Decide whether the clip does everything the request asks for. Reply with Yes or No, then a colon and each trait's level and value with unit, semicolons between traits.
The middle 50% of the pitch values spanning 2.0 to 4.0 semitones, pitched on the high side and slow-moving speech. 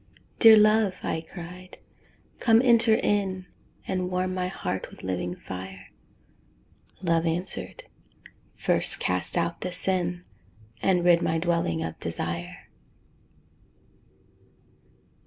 No: average, 2.8 semitones; medium, 180 Hz; slow, 105 wpm